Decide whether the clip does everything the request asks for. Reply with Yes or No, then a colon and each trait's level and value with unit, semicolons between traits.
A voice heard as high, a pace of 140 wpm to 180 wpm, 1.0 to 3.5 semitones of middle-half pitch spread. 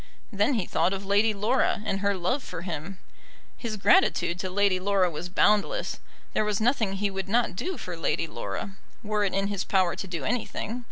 No: high, 200 Hz; average, 200 wpm; narrow, 2.5 semitones